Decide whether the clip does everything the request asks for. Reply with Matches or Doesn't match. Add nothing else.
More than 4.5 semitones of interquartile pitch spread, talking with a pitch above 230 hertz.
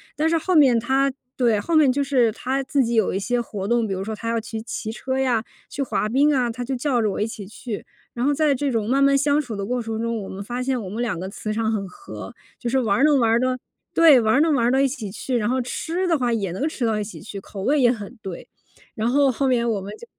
Doesn't match